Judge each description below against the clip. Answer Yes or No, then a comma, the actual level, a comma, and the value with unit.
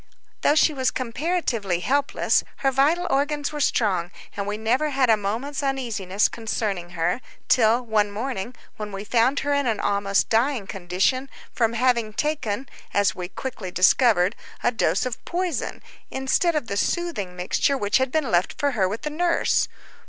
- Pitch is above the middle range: Yes, high, 235 Hz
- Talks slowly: No, average, 165 wpm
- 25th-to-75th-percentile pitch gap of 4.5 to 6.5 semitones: Yes, wide, 5.5 semitones